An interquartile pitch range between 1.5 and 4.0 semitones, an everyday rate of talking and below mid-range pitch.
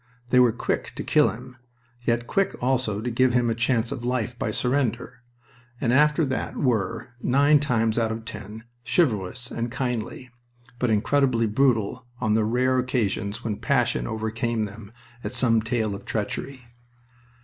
Yes: narrow, 2.5 semitones; average, 160 wpm; low, 120 Hz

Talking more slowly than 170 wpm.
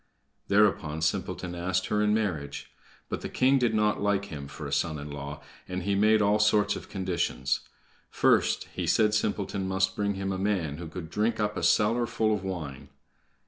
No: average, 190 wpm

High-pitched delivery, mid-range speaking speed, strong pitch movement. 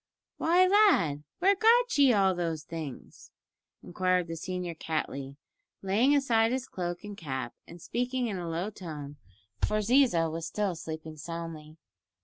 No: medium, 180 Hz; average, 145 wpm; wide, 7.1 semitones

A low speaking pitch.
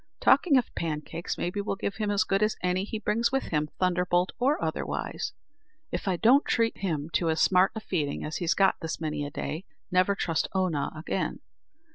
No: medium, 185 Hz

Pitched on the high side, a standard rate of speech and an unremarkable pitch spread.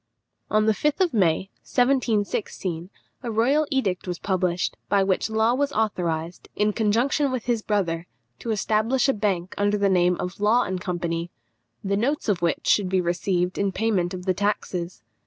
Yes: high, 200 Hz; average, 175 wpm; average, 3.8 semitones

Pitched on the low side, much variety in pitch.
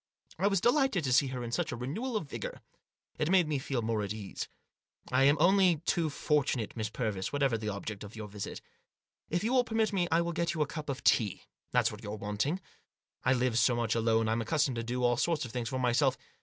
Yes: low, 130 Hz; wide, 6.7 semitones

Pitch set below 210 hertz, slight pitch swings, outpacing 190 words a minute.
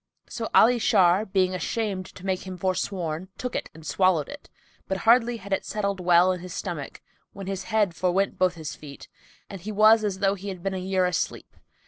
Yes: high, 190 Hz; narrow, 2.0 semitones; fast, 205 wpm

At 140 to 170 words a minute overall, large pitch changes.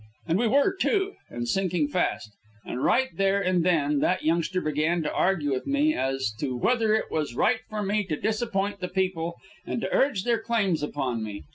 No: average, 200 wpm; wide, 6.6 semitones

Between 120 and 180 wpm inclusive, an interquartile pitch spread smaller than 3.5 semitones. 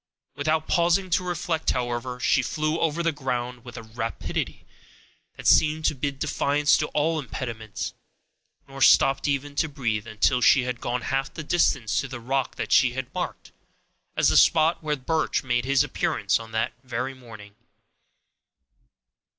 No: average, 160 wpm; average, 4.1 semitones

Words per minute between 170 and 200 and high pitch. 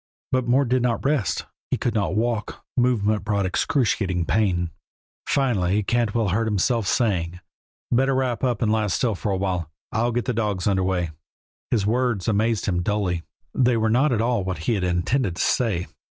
No: average, 180 wpm; low, 110 Hz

